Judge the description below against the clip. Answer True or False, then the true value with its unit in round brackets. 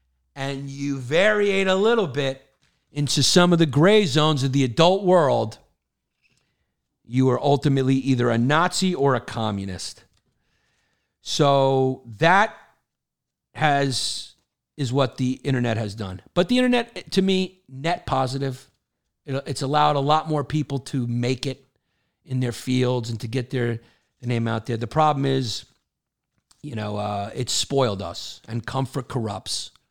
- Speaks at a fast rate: False (150 wpm)